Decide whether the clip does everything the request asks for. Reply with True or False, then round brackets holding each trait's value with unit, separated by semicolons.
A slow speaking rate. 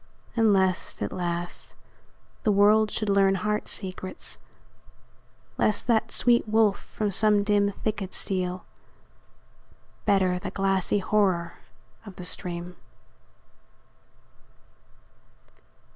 True (100 wpm)